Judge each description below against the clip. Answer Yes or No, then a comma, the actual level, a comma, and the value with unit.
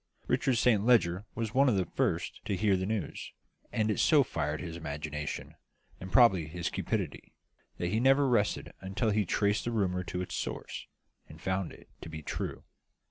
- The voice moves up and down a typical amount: Yes, average, 4.8 semitones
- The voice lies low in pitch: Yes, low, 100 Hz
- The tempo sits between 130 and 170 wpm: No, average, 190 wpm